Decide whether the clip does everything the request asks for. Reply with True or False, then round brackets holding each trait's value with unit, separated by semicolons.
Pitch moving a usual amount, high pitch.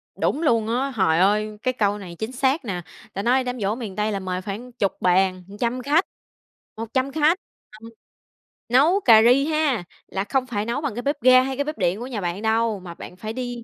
True (4.5 semitones; 230 Hz)